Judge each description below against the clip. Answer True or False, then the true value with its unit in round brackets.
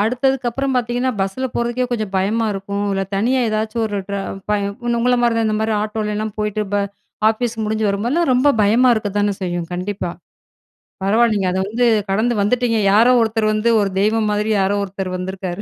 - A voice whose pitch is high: True (215 Hz)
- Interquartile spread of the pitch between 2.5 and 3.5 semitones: True (2.9 semitones)